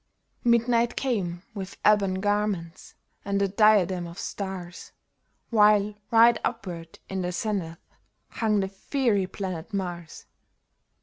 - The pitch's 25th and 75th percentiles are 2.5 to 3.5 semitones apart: Yes, average, 3.0 semitones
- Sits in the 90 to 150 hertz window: No, high, 200 Hz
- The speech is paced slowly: Yes, slow, 115 wpm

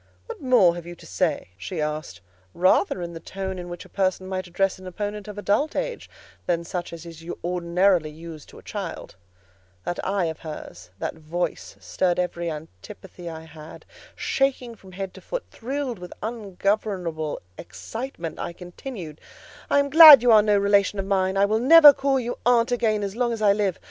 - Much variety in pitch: No, average, 4.4 semitones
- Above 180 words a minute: Yes, average, 190 wpm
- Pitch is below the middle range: No, high, 190 Hz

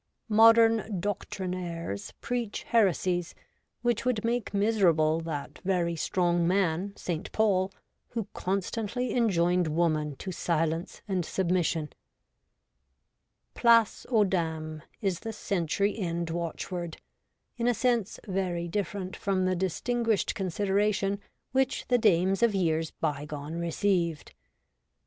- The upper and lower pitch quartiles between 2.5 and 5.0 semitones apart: Yes, average, 3.8 semitones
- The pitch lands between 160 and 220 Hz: Yes, medium, 185 Hz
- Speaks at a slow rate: Yes, slow, 110 wpm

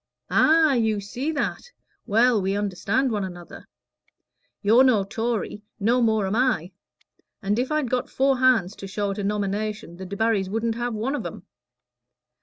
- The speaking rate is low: No, average, 165 wpm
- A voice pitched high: Yes, high, 220 Hz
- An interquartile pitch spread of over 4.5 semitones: No, average, 3.9 semitones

